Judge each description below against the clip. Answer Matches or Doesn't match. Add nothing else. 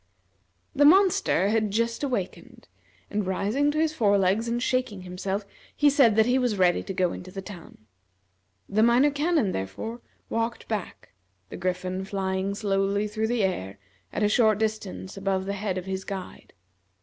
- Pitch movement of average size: Matches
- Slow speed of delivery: Doesn't match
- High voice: Matches